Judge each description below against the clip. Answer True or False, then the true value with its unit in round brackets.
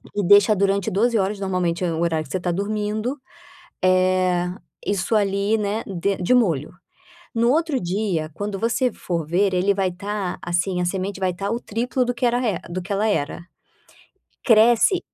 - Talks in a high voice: True (200 Hz)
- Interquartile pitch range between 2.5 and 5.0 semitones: True (3.3 semitones)